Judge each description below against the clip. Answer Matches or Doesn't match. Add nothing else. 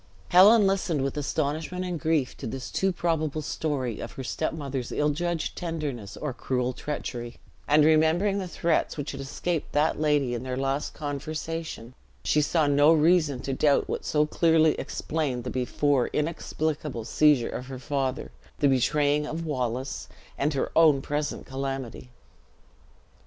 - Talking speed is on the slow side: Doesn't match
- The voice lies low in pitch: Doesn't match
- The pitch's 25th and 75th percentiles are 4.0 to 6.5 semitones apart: Doesn't match